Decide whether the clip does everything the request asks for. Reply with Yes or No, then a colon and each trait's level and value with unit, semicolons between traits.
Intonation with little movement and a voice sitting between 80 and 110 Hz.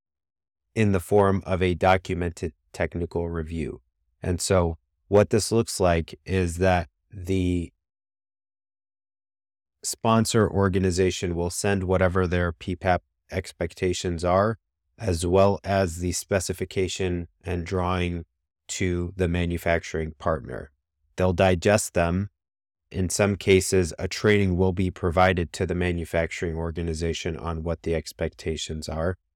Yes: narrow, 2.2 semitones; very low, 90 Hz